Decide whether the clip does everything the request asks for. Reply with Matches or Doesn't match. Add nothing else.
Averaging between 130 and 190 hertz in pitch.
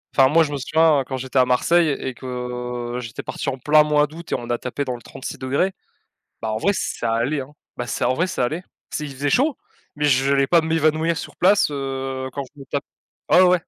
Matches